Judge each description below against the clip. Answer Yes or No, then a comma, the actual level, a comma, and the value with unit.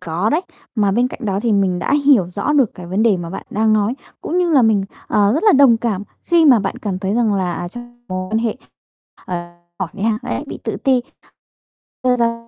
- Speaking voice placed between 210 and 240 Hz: Yes, high, 220 Hz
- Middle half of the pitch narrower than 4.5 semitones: Yes, average, 4.0 semitones